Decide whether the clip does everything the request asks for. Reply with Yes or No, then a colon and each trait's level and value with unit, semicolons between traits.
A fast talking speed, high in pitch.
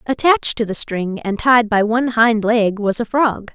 Yes: fast, 220 wpm; high, 225 Hz